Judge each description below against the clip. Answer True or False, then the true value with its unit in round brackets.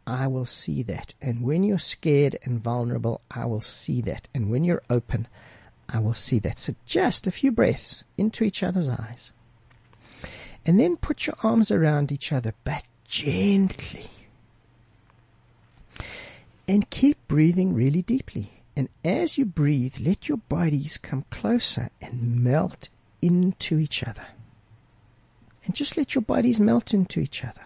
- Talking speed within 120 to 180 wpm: True (150 wpm)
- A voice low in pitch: True (130 Hz)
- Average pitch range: False (7.9 semitones)